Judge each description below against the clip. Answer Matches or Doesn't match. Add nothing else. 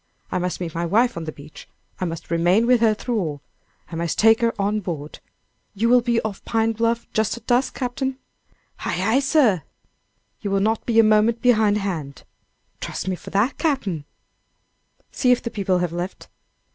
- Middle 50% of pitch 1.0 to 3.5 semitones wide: Doesn't match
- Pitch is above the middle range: Matches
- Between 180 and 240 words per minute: Matches